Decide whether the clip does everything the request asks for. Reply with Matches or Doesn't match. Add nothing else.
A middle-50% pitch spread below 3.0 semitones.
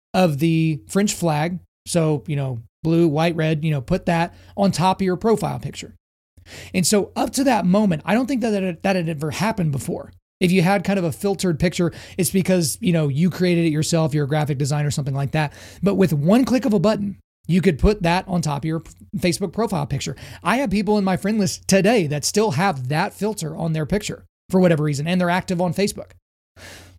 Doesn't match